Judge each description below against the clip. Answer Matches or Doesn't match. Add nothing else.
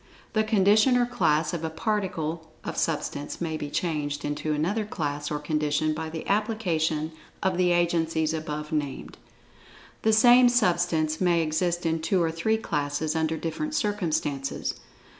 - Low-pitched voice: Doesn't match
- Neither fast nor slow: Matches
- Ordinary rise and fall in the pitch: Matches